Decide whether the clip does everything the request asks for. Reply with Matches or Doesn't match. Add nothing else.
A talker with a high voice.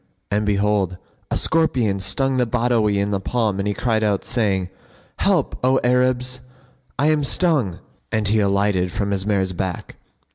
Doesn't match